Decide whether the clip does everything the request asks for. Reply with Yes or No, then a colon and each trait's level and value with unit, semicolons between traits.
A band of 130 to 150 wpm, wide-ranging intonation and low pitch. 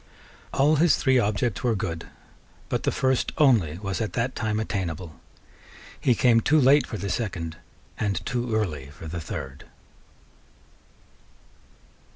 Yes: average, 140 wpm; wide, 6.5 semitones; low, 110 Hz